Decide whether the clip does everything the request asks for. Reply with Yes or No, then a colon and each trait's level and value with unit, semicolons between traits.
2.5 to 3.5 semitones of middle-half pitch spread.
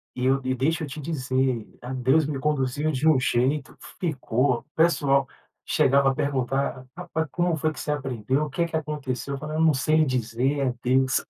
Yes: average, 2.9 semitones